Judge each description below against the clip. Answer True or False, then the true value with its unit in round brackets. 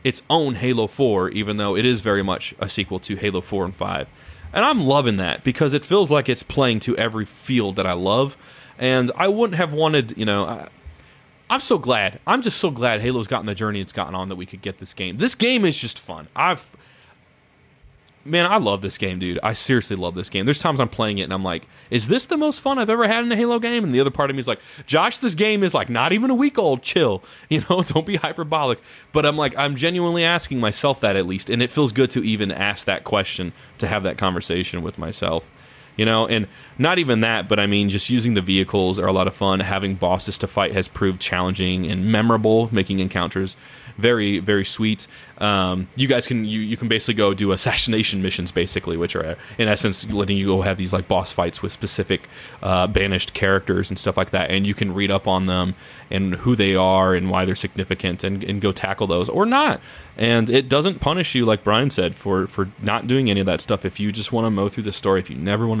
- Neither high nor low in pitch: False (105 Hz)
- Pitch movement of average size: False (5.7 semitones)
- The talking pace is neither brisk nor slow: False (240 wpm)